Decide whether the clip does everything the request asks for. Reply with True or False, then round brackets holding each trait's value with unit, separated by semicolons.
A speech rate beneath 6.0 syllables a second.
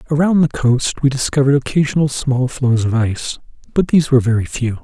False (6.1 syllables/s)